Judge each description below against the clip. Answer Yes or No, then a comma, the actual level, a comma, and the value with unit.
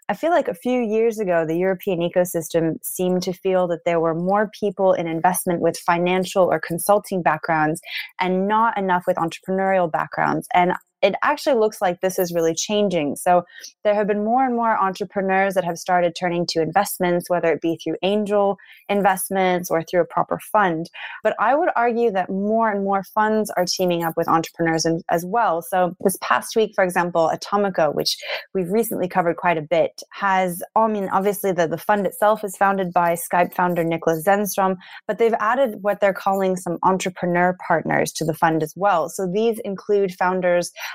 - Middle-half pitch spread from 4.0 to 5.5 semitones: No, average, 2.8 semitones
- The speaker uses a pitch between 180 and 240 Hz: Yes, medium, 185 Hz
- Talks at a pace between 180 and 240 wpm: Yes, average, 190 wpm